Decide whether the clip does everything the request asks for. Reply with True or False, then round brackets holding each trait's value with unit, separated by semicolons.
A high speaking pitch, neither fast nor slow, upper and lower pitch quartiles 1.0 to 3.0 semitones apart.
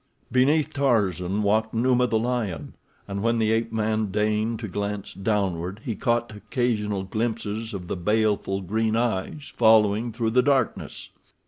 False (110 Hz; 145 wpm; 2.5 semitones)